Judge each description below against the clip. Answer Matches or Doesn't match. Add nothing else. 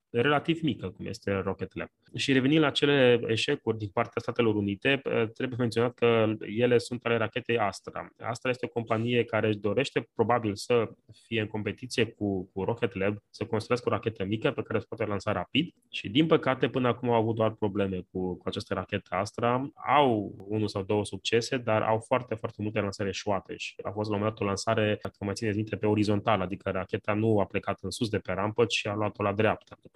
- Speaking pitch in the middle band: Doesn't match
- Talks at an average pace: Doesn't match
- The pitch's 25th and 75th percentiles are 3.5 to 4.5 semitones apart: Doesn't match